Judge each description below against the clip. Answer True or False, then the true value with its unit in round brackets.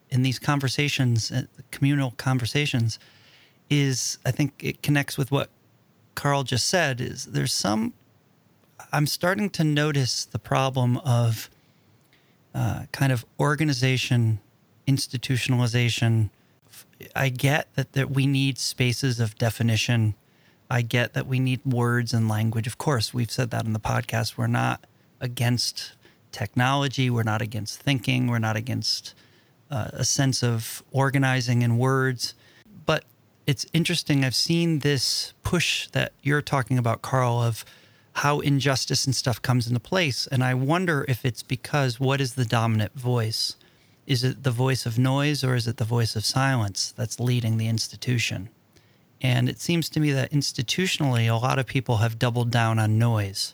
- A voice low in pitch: True (130 Hz)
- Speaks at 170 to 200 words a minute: False (155 wpm)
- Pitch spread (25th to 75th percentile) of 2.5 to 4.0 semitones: True (2.8 semitones)